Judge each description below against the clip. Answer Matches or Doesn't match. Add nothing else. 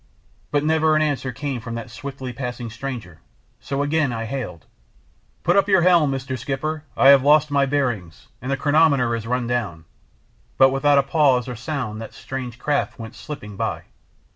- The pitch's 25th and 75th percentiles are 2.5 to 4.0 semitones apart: Matches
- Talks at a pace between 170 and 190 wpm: Matches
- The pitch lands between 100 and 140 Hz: Matches